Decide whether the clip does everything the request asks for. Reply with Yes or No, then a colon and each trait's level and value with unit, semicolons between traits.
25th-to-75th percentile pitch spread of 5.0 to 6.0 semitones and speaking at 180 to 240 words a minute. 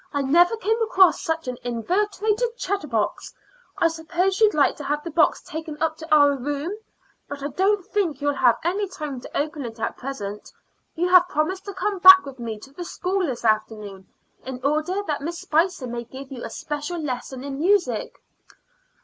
Yes: wide, 5.5 semitones; average, 190 wpm